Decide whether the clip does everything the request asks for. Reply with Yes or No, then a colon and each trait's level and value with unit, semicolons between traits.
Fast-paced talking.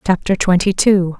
No: average, 150 wpm